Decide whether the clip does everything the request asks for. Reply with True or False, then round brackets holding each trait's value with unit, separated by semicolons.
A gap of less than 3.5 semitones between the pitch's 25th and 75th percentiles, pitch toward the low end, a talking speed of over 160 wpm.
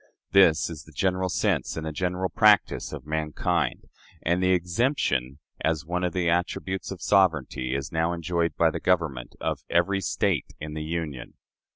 True (3.0 semitones; 85 Hz; 170 wpm)